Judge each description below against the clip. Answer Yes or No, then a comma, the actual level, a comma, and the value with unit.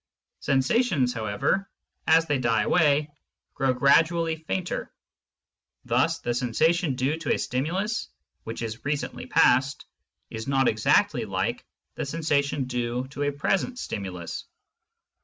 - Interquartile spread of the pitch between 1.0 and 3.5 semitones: No, average, 4.7 semitones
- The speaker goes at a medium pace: No, slow, 120 wpm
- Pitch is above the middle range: No, medium, 140 Hz